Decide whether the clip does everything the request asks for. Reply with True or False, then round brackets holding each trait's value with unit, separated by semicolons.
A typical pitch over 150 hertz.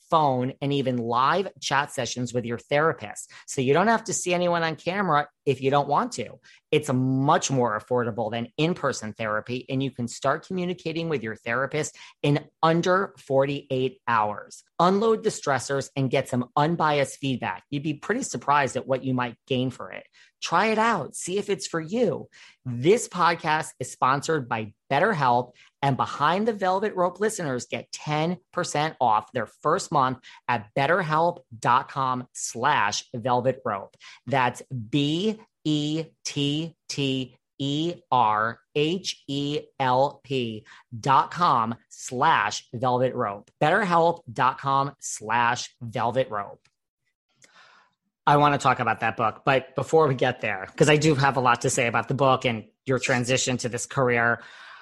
False (140 Hz)